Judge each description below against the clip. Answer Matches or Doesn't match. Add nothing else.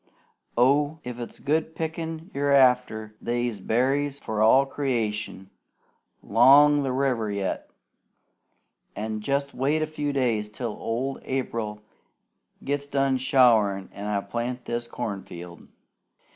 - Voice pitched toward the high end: Doesn't match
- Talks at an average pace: Doesn't match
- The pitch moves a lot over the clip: Doesn't match